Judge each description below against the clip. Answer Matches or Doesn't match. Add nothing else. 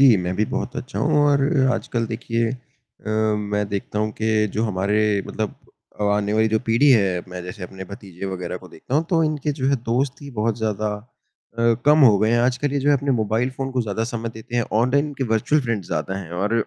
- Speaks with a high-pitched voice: Doesn't match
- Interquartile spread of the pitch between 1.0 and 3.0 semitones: Doesn't match